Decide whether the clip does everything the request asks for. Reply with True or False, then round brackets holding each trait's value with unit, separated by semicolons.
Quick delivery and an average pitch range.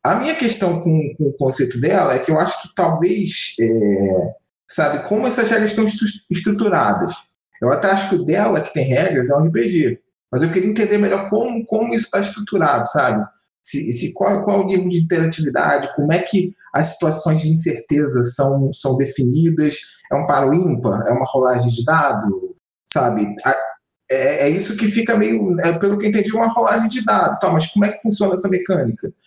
False (200 wpm; 6.1 semitones)